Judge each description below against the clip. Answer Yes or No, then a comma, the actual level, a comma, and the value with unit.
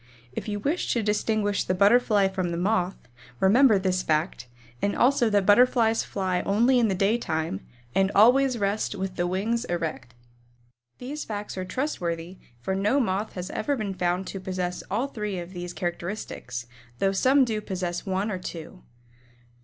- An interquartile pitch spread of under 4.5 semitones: Yes, average, 3.5 semitones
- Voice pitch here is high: Yes, high, 195 Hz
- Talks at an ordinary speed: Yes, average, 165 wpm